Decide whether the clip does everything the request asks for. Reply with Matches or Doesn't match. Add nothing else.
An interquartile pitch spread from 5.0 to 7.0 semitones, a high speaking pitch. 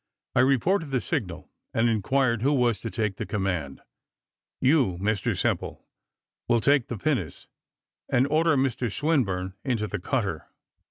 Doesn't match